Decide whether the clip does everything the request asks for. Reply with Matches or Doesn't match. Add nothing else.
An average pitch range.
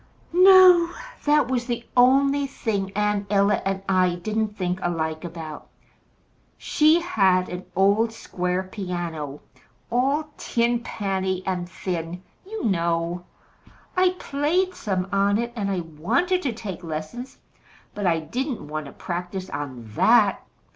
Doesn't match